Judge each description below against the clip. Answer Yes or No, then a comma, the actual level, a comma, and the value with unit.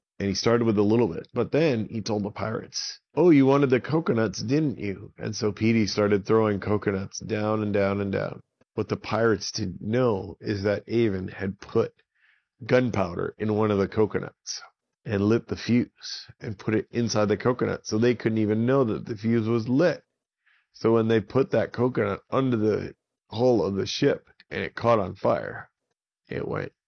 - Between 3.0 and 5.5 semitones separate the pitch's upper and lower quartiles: No, narrow, 2.5 semitones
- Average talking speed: Yes, average, 190 wpm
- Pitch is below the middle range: Yes, low, 110 Hz